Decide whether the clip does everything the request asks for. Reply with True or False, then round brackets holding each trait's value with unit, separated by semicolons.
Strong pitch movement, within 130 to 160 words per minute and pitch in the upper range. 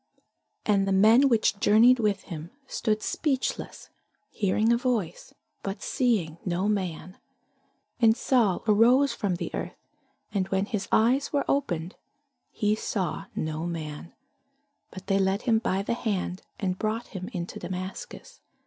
False (3.8 semitones; 140 wpm; 200 Hz)